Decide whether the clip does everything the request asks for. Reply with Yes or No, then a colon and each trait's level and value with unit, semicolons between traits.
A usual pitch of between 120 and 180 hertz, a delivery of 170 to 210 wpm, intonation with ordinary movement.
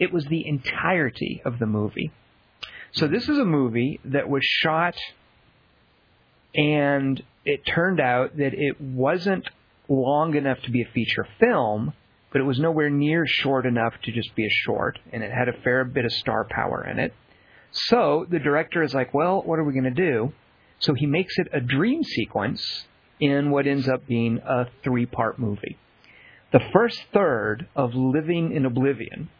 Yes: medium, 140 Hz; average, 180 wpm; average, 4.0 semitones